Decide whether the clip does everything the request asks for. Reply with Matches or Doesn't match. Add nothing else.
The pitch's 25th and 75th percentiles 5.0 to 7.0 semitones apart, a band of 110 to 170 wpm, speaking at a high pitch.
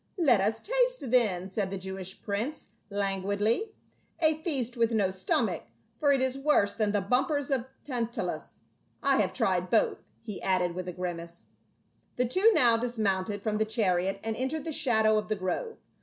Doesn't match